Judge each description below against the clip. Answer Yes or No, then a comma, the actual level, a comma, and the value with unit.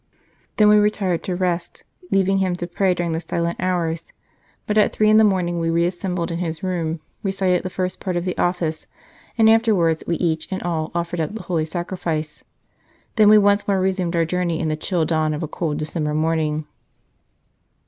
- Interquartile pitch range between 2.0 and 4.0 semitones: Yes, narrow, 2.6 semitones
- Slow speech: No, average, 195 wpm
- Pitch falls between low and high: Yes, medium, 175 Hz